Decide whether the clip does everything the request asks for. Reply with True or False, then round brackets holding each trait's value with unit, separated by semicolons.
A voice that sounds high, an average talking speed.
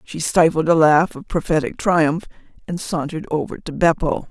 False (165 Hz; 165 wpm)